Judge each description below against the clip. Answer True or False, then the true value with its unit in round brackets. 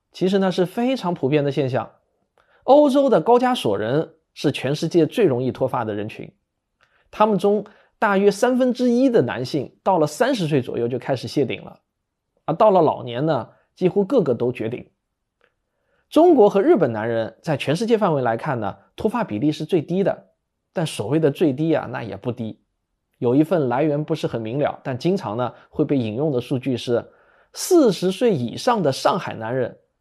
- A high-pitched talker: False (155 Hz)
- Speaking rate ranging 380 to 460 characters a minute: False (270 characters per minute)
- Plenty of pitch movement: True (8.2 semitones)